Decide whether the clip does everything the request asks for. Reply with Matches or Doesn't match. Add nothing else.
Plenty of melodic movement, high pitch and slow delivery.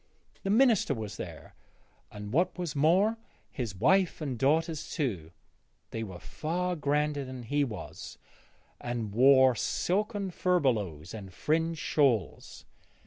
Doesn't match